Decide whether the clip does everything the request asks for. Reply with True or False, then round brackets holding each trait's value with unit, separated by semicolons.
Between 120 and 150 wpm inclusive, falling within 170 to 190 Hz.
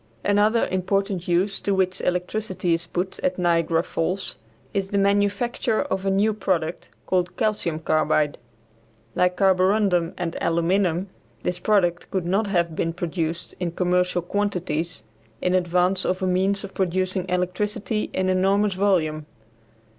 True (140 wpm; 185 Hz)